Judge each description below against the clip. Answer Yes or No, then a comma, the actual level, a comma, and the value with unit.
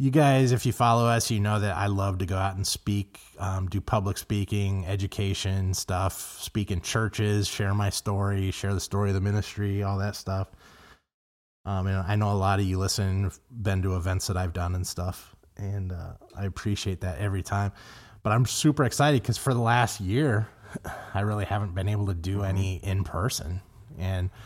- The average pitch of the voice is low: Yes, low, 100 Hz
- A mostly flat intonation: Yes, narrow, 1.8 semitones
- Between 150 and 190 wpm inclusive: No, average, 200 wpm